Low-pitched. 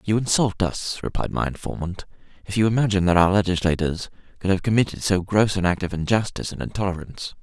Yes: very low, 95 Hz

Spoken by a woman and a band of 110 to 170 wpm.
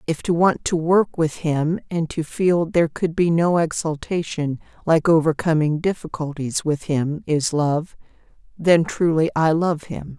Yes: female; average, 160 wpm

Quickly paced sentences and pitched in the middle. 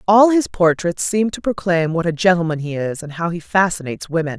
Yes: fast, 220 wpm; medium, 175 Hz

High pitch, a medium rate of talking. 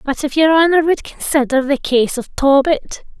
Yes: very high, 285 Hz; average, 190 wpm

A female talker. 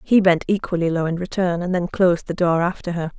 Yes: female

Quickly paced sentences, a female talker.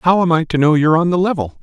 No: fast, 330 wpm; male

